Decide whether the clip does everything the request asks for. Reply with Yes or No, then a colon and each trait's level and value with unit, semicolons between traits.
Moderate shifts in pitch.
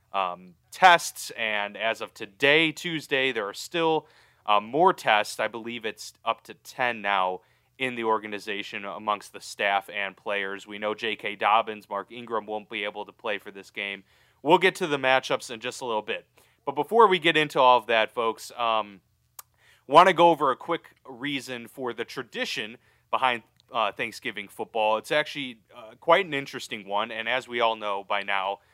Yes: average, 4.3 semitones